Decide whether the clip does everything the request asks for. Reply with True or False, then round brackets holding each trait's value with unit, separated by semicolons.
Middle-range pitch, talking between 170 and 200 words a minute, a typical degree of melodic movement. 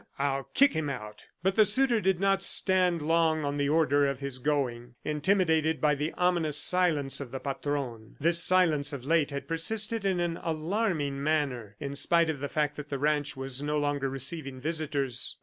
True (150 Hz; 185 wpm; 3.4 semitones)